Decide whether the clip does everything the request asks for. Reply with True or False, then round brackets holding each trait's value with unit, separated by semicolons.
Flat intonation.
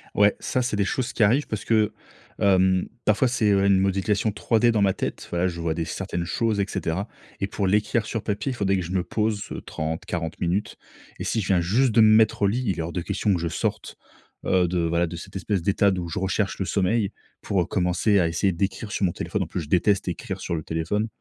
False (3.2 semitones)